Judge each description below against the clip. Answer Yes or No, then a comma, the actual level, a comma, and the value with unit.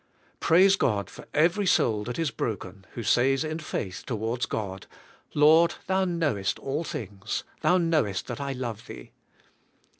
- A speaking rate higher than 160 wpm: No, average, 150 wpm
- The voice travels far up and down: Yes, wide, 7.5 semitones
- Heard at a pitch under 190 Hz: Yes, low, 135 Hz